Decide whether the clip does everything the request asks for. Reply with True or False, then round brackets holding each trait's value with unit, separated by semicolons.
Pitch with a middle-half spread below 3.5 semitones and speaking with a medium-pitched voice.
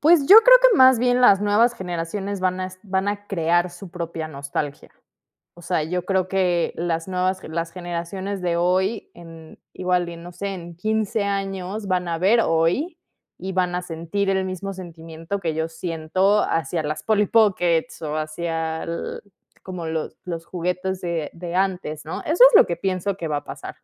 True (2.9 semitones; 180 Hz)